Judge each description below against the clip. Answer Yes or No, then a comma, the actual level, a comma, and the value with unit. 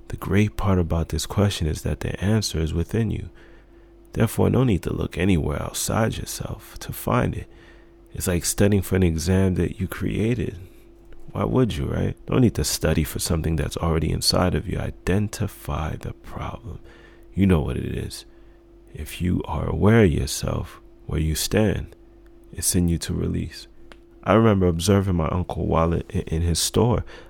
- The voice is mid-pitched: No, very low, 90 Hz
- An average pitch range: Yes, average, 3.9 semitones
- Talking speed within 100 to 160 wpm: No, average, 175 wpm